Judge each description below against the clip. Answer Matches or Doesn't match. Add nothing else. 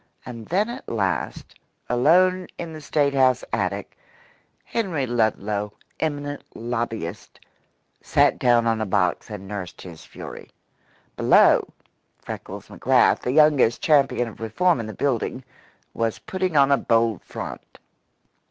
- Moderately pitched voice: Doesn't match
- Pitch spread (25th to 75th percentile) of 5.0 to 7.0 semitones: Matches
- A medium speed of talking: Doesn't match